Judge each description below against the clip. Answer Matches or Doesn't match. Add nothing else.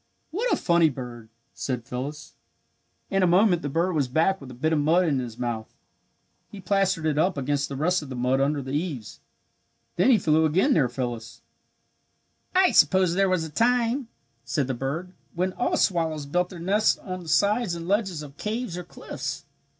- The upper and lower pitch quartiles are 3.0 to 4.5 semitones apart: Doesn't match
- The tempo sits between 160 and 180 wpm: Doesn't match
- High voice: Doesn't match